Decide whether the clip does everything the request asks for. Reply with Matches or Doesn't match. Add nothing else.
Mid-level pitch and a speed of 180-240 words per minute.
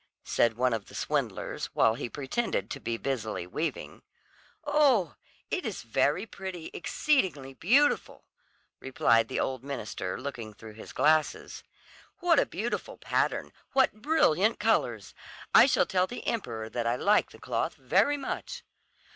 Doesn't match